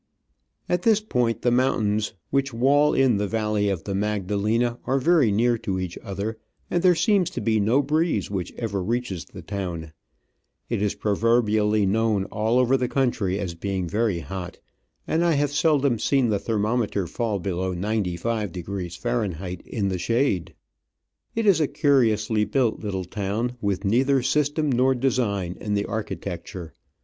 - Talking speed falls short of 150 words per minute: No, average, 165 wpm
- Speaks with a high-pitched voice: No, low, 110 Hz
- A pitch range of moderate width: Yes, average, 4.6 semitones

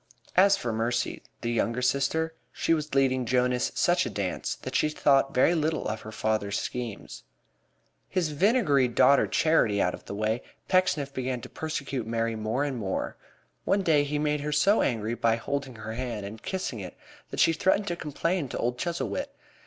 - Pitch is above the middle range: No, low, 135 Hz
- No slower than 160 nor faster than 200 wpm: Yes, average, 185 wpm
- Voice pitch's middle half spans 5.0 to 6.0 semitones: Yes, average, 5.3 semitones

